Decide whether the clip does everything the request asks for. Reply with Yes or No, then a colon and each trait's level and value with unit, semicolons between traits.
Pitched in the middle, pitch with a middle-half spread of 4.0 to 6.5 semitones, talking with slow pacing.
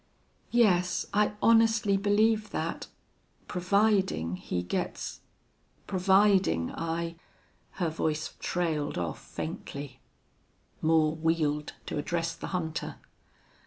Yes: medium, 170 Hz; average, 4.7 semitones; slow, 95 wpm